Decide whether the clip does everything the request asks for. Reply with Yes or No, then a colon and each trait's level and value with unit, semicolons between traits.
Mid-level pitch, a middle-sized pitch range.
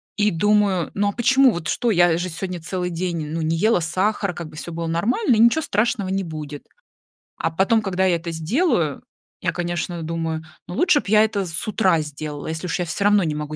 Yes: medium, 175 Hz; average, 4.2 semitones